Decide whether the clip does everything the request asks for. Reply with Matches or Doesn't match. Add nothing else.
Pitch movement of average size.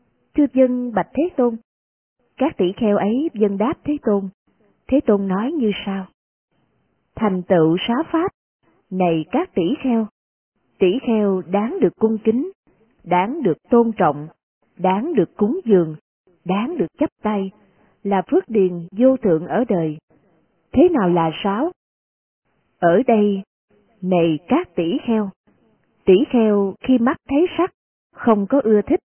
Doesn't match